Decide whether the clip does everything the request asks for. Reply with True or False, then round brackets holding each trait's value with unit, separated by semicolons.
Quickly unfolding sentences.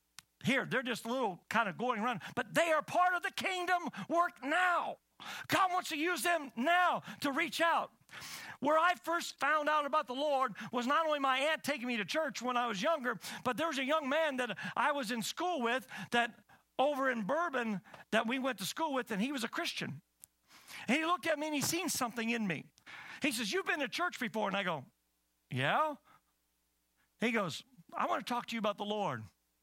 True (220 wpm)